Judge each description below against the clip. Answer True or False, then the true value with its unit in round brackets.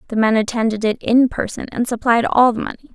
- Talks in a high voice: True (230 Hz)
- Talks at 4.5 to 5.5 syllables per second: False (6.0 syllables/s)